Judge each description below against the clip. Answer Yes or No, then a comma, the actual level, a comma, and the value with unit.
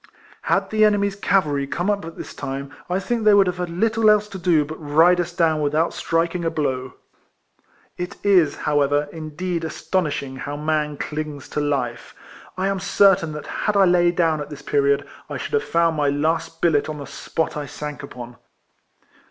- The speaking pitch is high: No, medium, 160 Hz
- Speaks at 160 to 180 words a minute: No, average, 190 wpm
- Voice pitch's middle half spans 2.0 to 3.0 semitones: No, average, 3.8 semitones